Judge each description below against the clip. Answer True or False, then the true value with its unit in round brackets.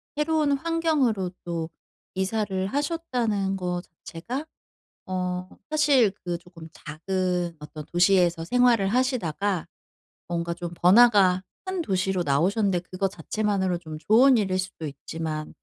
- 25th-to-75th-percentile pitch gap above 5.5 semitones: False (5.2 semitones)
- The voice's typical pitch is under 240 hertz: True (190 Hz)